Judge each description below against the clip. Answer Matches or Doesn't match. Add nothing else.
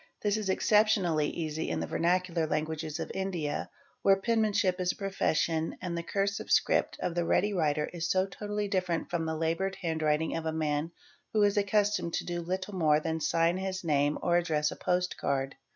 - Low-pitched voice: Doesn't match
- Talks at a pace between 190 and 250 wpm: Matches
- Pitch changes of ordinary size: Matches